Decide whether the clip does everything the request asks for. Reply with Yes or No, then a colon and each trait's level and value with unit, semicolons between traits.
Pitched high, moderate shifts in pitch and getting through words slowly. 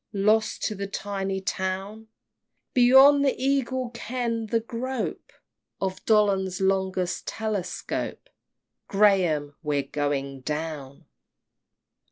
Yes: high, 195 Hz; average, 4.4 semitones; slow, 95 wpm